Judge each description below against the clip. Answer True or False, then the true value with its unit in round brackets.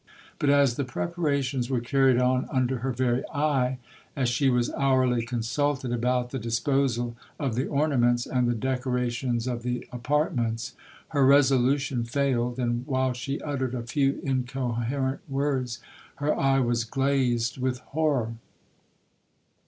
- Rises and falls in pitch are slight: True (2.2 semitones)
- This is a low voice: True (130 Hz)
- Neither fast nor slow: False (130 wpm)